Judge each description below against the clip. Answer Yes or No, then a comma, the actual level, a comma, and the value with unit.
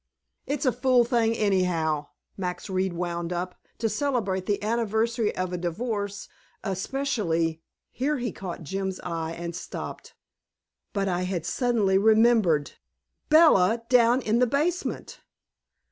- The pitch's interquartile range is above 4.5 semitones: Yes, average, 4.9 semitones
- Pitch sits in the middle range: No, high, 200 Hz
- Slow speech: Yes, slow, 130 wpm